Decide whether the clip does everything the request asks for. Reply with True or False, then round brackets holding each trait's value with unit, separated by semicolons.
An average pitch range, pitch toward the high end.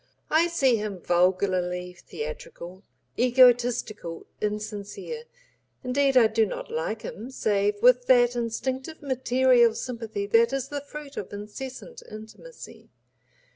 True (4.2 semitones; 235 Hz)